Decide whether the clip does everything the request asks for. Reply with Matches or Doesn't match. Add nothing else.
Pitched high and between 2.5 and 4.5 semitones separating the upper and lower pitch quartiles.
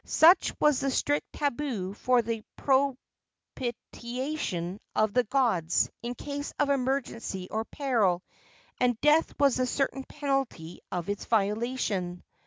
Doesn't match